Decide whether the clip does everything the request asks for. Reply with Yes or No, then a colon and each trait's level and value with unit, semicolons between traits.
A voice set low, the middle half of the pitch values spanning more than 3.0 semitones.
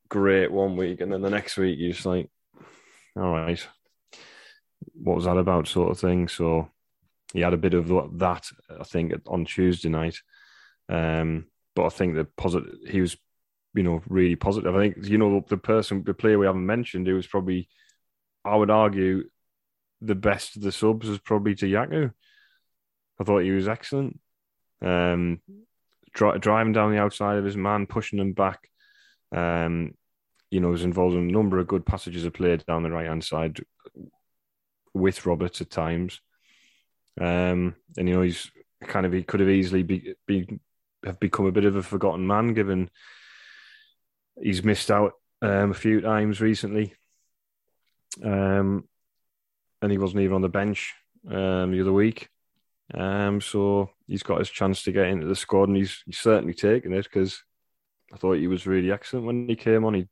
No: very low, 95 Hz; narrow, 2.5 semitones